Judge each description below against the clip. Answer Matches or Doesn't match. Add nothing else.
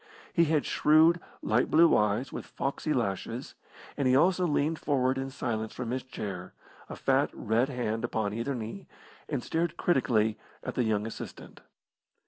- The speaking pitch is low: Matches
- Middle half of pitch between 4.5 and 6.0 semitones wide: Matches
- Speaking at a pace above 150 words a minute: Matches